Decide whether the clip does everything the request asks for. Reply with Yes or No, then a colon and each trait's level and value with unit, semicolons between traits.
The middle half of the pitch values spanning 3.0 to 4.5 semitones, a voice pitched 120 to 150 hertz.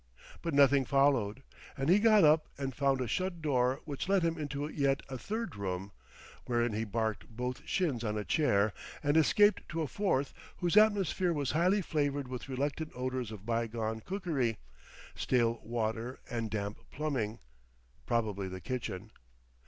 No: wide, 5.5 semitones; low, 135 Hz